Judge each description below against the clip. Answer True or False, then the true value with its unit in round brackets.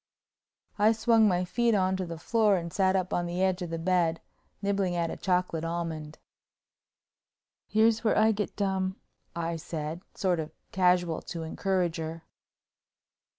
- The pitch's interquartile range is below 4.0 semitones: True (2.9 semitones)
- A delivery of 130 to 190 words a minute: True (155 wpm)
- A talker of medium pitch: True (180 Hz)